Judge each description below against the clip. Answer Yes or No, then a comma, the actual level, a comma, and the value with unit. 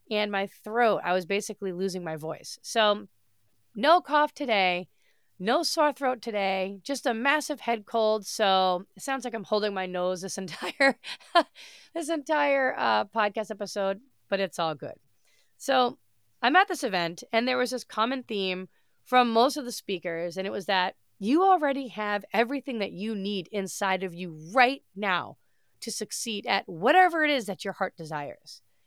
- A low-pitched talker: No, high, 210 Hz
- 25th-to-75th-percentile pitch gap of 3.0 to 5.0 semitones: No, wide, 5.4 semitones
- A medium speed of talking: Yes, average, 175 wpm